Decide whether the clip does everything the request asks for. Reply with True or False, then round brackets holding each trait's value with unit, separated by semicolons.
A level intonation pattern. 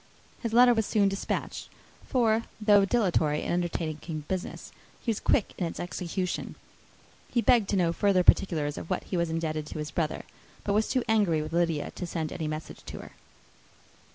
False (4.6 semitones)